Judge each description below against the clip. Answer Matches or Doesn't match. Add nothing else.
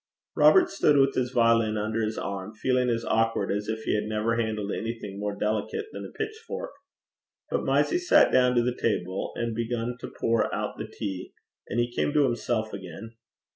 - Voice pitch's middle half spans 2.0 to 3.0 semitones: Matches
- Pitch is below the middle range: Matches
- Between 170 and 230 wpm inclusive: Matches